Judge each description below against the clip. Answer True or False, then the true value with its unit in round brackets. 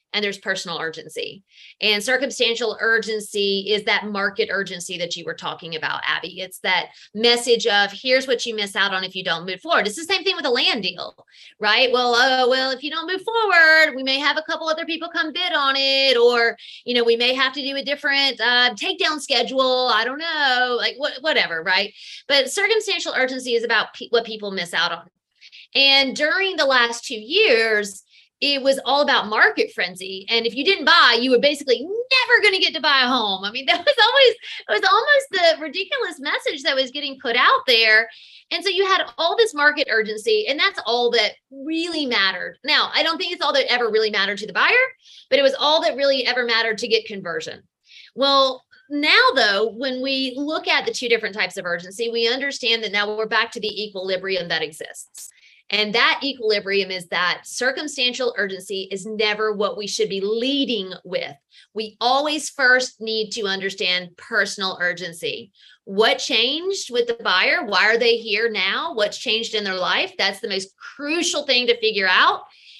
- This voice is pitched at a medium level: False (245 Hz)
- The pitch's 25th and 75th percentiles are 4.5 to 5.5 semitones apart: False (6.0 semitones)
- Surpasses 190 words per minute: True (200 wpm)